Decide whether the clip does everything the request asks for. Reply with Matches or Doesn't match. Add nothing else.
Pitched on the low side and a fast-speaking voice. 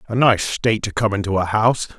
Matches